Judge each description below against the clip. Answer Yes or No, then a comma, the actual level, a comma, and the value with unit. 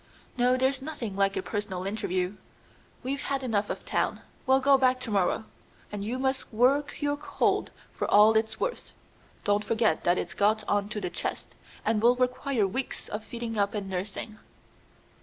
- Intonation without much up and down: No, average, 4.2 semitones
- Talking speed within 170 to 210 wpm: Yes, average, 175 wpm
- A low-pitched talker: No, high, 220 Hz